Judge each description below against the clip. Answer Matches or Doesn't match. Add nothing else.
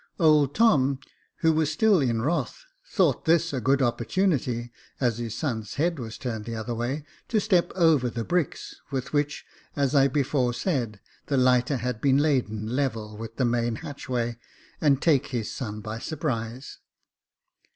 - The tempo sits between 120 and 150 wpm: Doesn't match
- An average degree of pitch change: Matches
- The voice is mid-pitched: Doesn't match